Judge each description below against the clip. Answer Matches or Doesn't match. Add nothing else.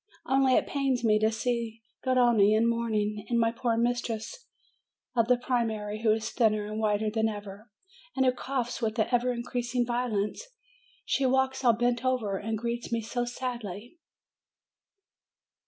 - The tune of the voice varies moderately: Doesn't match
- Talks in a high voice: Matches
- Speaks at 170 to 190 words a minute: Doesn't match